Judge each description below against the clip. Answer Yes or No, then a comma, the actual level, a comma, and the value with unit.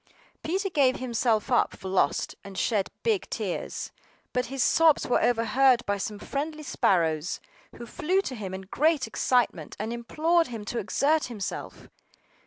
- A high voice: Yes, high, 245 Hz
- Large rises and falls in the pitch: Yes, wide, 6.5 semitones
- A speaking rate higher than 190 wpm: No, average, 155 wpm